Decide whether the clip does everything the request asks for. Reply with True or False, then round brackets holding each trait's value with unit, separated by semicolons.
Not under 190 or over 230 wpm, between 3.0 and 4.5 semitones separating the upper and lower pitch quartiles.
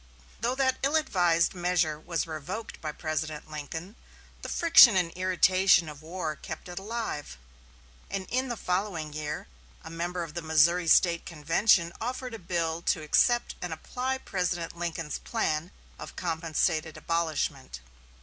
False (145 wpm; 3.4 semitones)